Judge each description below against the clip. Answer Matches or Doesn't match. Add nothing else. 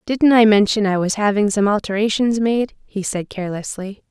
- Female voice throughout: Matches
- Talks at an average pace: Matches